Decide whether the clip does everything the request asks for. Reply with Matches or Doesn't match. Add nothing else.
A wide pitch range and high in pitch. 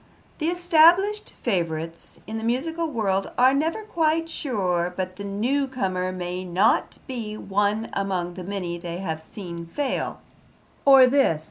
Matches